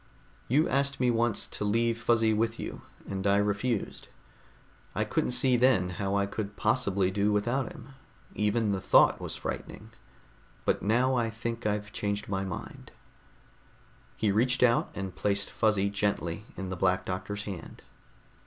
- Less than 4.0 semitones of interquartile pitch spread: Yes, average, 2.9 semitones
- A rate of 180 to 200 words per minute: No, average, 155 wpm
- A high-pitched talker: No, low, 105 Hz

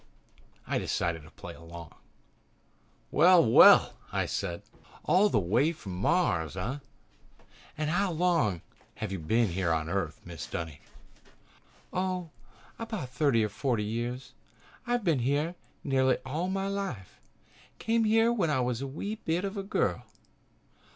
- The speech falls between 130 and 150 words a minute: Yes, average, 140 wpm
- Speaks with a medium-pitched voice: No, low, 130 Hz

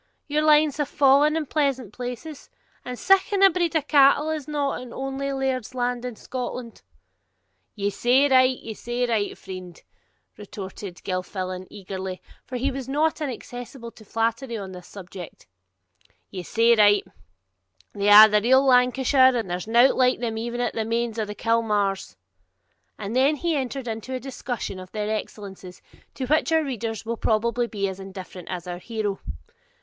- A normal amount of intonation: Yes, average, 4.6 semitones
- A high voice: Yes, high, 240 Hz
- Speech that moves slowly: No, average, 170 wpm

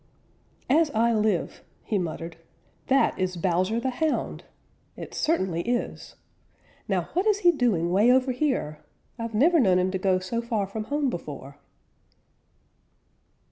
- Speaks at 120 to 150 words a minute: Yes, average, 140 wpm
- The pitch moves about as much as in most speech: No, wide, 6.2 semitones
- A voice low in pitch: No, high, 220 Hz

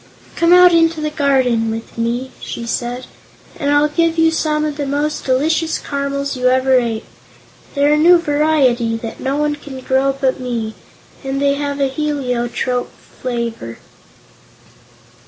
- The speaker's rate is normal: Yes, average, 155 wpm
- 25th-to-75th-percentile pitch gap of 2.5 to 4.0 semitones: Yes, average, 3.3 semitones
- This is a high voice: Yes, very high, 275 Hz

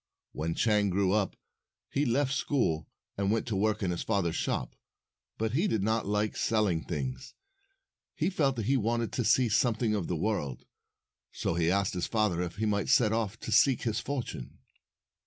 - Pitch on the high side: No, low, 105 Hz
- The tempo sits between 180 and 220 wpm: Yes, average, 185 wpm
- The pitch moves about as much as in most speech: Yes, average, 3.5 semitones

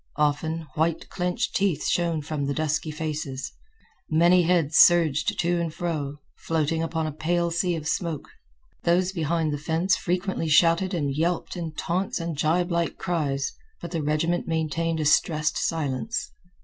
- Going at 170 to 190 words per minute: No, average, 150 wpm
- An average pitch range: No, narrow, 2.1 semitones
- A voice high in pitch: No, medium, 165 Hz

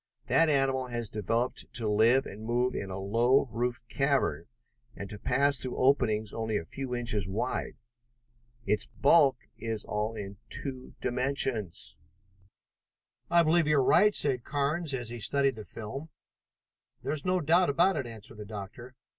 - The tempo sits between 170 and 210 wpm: No, average, 160 wpm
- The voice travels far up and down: No, average, 4.4 semitones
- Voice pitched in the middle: No, low, 125 Hz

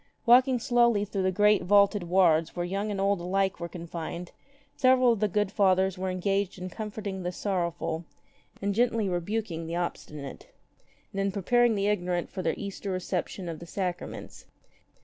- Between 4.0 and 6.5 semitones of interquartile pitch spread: No, average, 2.8 semitones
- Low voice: No, high, 195 Hz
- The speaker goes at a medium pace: Yes, average, 170 wpm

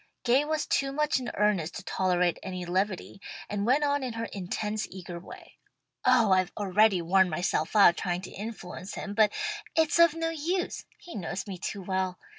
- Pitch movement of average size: No, wide, 5.8 semitones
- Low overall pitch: No, high, 200 Hz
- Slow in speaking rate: No, average, 185 wpm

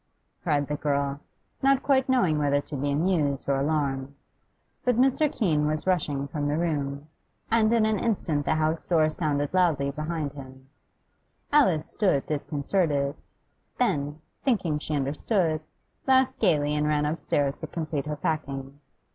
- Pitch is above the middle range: No, medium, 150 Hz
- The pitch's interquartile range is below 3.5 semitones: No, average, 3.8 semitones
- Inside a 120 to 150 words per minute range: Yes, average, 145 wpm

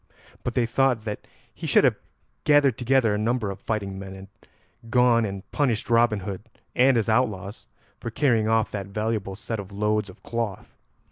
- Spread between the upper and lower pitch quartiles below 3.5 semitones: Yes, average, 3.0 semitones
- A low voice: Yes, low, 110 Hz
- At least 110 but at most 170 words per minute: No, average, 180 wpm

